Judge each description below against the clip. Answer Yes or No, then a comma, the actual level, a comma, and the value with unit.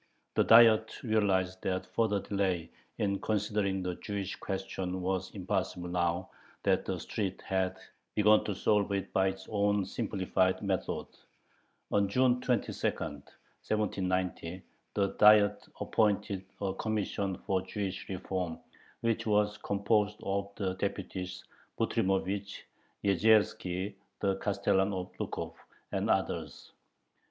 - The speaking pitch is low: Yes, low, 100 Hz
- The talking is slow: Yes, slow, 115 wpm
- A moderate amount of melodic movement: No, narrow, 1.9 semitones